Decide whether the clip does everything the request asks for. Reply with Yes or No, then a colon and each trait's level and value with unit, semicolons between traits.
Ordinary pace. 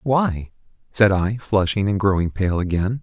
Yes: average, 160 wpm